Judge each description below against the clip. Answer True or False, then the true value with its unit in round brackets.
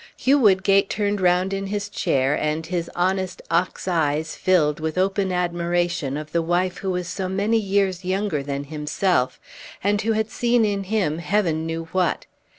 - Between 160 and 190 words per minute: True (170 wpm)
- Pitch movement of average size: True (3.4 semitones)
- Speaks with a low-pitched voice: False (185 Hz)